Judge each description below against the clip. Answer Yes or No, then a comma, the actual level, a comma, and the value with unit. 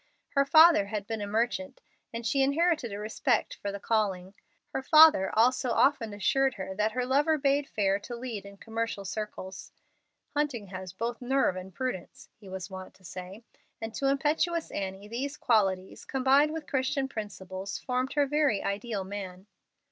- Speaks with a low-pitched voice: No, high, 225 Hz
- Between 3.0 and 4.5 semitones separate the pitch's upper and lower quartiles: No, wide, 5.5 semitones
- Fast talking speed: No, average, 170 wpm